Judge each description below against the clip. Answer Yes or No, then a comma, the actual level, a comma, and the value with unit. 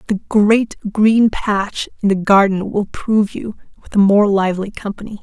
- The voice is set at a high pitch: Yes, high, 205 Hz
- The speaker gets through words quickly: No, average, 170 wpm